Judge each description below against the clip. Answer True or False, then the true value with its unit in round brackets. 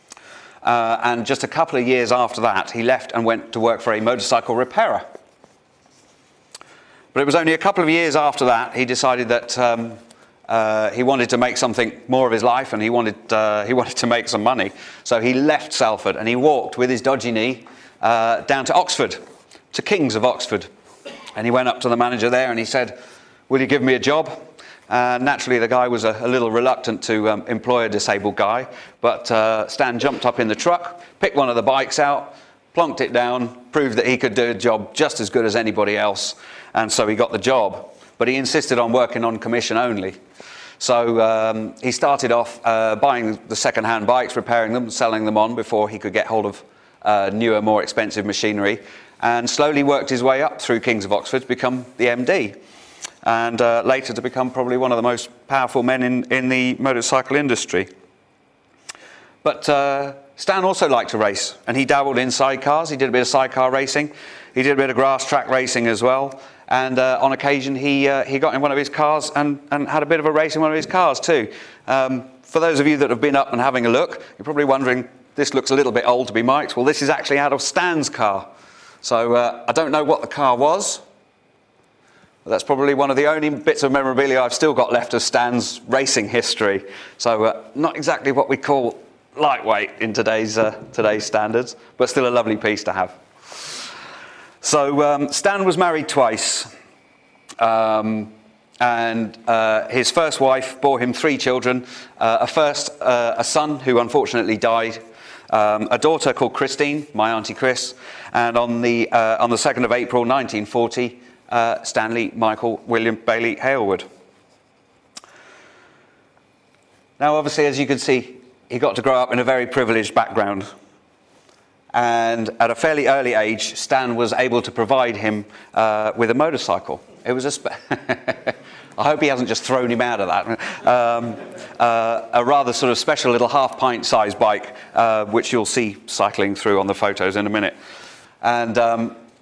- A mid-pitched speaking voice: False (125 Hz)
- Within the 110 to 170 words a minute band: False (200 wpm)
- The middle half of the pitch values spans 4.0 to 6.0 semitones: False (3.0 semitones)